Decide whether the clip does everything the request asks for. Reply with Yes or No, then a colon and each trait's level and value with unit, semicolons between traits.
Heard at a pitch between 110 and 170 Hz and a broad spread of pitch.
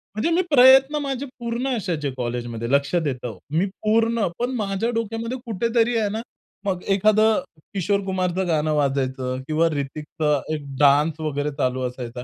No: medium, 180 Hz; wide, 8.2 semitones